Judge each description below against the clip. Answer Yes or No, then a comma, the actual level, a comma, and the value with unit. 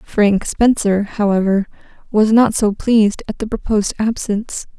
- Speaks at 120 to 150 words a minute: Yes, average, 140 wpm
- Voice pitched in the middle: No, high, 210 Hz